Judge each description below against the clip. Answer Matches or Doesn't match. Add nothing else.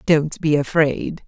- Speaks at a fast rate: Doesn't match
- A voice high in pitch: Doesn't match